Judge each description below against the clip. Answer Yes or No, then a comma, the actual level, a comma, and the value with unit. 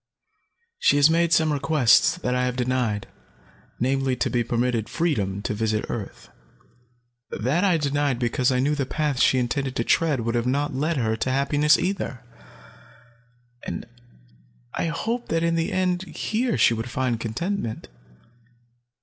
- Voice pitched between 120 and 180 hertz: Yes, low, 135 Hz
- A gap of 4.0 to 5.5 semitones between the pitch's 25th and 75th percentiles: Yes, average, 5.1 semitones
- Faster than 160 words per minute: No, average, 155 wpm